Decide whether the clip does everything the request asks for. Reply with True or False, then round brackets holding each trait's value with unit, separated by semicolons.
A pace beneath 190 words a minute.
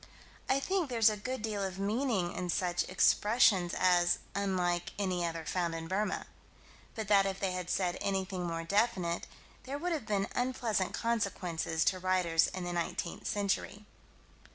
True (160 wpm)